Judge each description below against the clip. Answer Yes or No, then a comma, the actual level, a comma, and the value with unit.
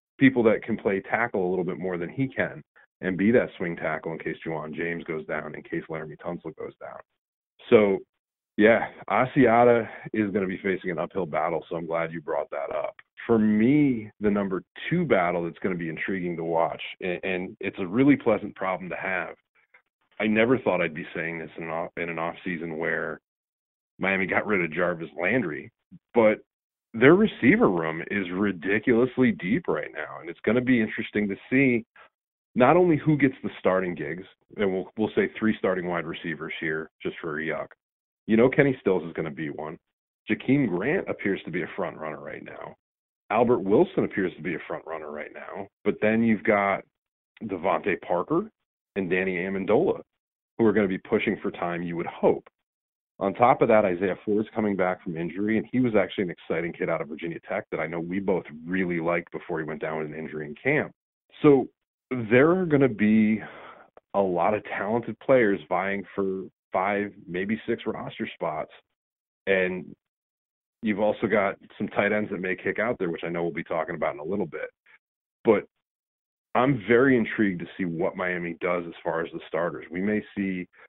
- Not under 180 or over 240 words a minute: Yes, average, 200 wpm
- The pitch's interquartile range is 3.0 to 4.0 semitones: No, average, 4.7 semitones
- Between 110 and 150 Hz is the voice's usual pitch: No, very low, 95 Hz